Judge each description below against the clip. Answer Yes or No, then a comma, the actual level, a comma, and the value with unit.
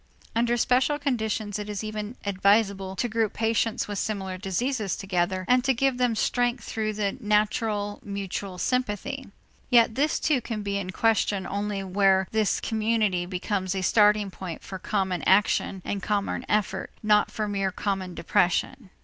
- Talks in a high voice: Yes, high, 210 Hz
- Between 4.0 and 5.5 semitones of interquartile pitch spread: No, average, 2.8 semitones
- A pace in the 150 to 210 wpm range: Yes, average, 160 wpm